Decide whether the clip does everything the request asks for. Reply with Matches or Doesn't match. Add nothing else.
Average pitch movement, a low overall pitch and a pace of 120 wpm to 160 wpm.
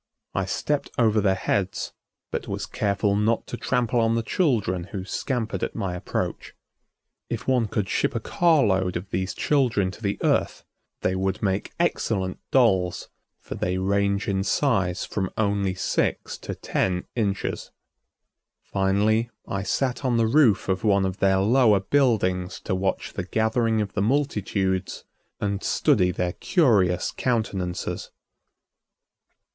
Matches